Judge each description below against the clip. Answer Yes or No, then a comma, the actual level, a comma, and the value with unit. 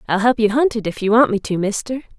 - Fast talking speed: Yes, fast, 300 wpm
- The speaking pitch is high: Yes, high, 220 Hz